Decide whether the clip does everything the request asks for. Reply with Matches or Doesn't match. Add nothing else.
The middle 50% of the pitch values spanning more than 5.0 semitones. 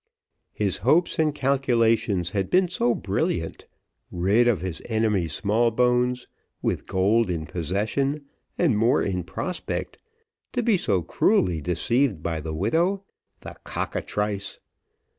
Matches